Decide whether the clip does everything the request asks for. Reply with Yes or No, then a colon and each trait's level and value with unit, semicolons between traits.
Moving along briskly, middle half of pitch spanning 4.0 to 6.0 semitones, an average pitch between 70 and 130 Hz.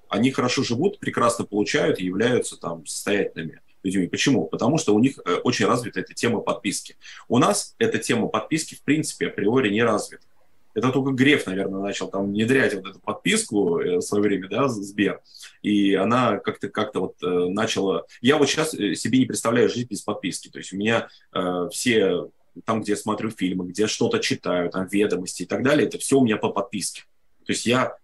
Yes: fast, 190 wpm; average, 5.0 semitones; low, 105 Hz